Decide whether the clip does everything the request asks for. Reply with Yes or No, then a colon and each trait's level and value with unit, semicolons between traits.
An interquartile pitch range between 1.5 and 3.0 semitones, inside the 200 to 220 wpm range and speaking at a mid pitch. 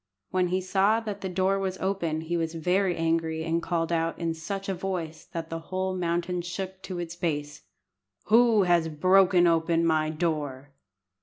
No: narrow, 2.5 semitones; average, 175 wpm; medium, 175 Hz